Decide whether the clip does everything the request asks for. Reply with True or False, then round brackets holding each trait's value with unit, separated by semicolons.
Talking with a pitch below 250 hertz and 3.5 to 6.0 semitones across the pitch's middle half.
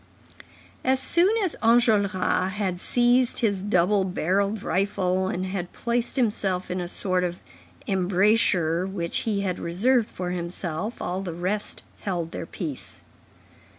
False (190 Hz; 3.0 semitones)